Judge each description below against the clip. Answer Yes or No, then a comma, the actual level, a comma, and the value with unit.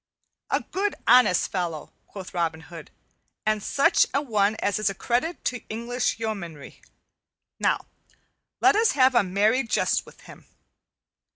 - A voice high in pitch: Yes, high, 215 Hz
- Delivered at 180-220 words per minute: No, average, 145 wpm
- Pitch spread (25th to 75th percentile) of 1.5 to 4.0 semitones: No, wide, 5.4 semitones